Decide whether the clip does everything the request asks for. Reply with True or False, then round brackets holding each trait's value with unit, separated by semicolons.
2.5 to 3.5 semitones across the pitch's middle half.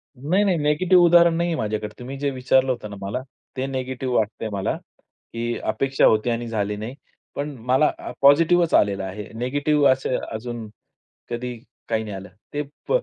False (5.0 semitones)